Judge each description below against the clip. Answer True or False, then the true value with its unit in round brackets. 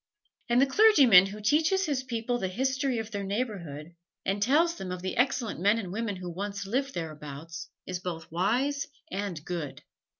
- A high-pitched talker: True (205 Hz)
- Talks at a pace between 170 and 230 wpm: True (175 wpm)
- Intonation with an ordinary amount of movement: False (6.3 semitones)